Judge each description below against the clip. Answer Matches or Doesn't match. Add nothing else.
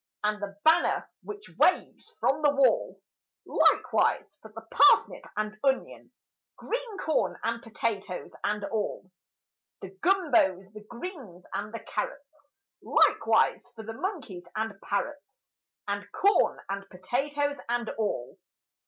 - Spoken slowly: Matches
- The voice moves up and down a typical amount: Doesn't match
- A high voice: Matches